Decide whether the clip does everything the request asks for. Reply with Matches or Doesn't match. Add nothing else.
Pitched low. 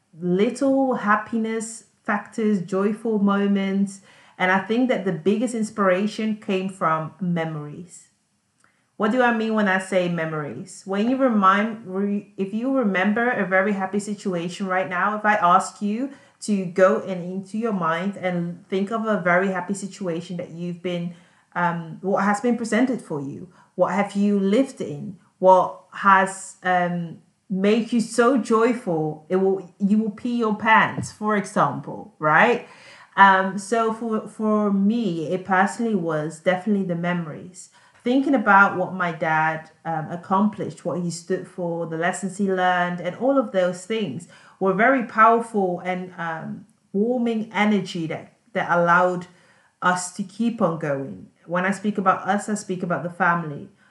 Doesn't match